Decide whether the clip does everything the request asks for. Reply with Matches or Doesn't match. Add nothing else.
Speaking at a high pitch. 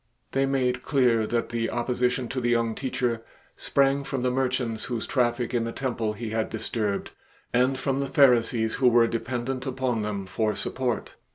Doesn't match